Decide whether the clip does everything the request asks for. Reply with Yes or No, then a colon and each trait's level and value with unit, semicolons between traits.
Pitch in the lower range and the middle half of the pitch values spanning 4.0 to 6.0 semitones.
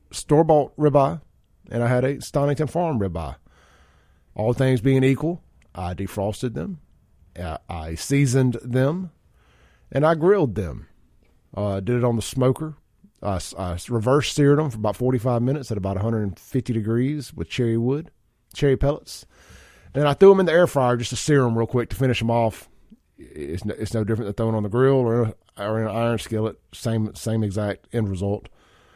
Yes: low, 115 Hz; average, 5.1 semitones